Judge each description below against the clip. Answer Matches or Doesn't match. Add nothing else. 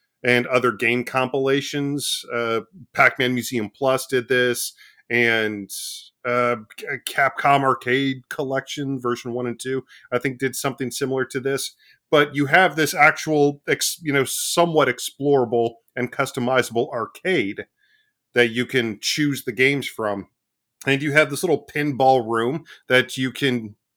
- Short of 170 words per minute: Matches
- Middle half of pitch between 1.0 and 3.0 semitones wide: Matches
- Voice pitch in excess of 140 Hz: Doesn't match